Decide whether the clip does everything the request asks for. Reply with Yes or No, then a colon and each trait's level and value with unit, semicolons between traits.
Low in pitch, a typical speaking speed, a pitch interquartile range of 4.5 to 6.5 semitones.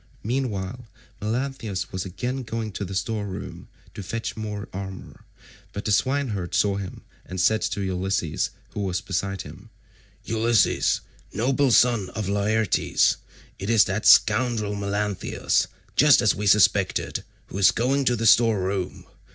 No: low, 105 Hz; average, 145 wpm; average, 3.0 semitones